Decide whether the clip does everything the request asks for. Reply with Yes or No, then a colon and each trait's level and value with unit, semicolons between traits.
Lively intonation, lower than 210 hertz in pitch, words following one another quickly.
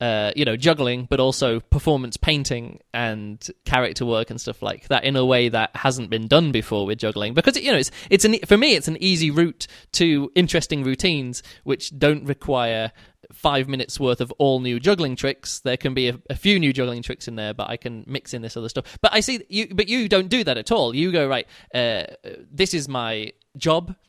Yes: wide, 6.0 semitones; low, 135 Hz; fast, 220 wpm